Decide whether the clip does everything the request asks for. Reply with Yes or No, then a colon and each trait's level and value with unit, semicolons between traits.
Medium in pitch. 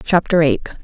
Yes: medium, 170 Hz